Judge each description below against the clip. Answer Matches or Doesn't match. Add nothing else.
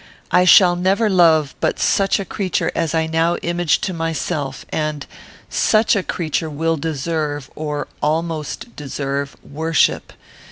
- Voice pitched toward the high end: Doesn't match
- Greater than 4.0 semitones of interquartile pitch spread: Doesn't match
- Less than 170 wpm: Matches